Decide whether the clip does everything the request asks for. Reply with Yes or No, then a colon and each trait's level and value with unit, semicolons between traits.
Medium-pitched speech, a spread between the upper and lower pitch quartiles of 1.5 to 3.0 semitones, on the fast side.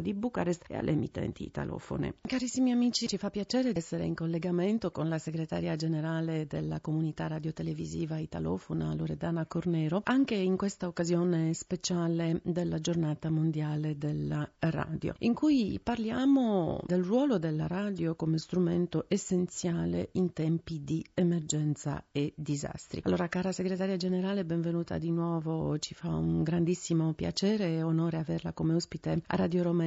No: medium, 170 Hz; average, 2.7 semitones; average, 140 wpm